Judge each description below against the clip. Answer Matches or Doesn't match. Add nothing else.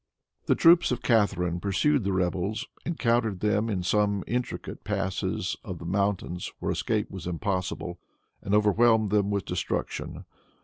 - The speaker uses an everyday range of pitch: Matches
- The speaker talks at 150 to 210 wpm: Doesn't match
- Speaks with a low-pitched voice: Matches